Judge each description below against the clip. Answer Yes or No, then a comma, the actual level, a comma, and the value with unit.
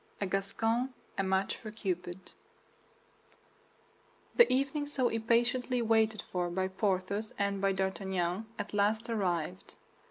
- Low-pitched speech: No, high, 200 Hz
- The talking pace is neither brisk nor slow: No, slow, 120 wpm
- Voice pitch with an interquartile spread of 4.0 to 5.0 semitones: No, average, 3.4 semitones